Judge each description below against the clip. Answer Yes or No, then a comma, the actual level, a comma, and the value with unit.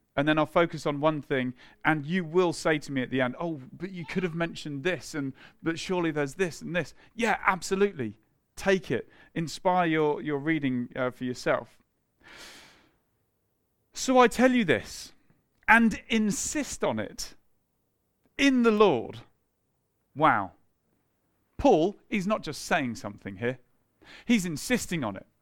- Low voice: No, medium, 165 Hz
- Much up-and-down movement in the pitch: Yes, wide, 6.1 semitones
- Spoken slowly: No, average, 155 wpm